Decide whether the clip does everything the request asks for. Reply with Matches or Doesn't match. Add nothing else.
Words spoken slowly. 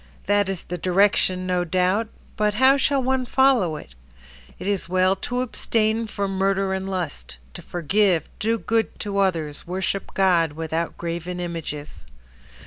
Doesn't match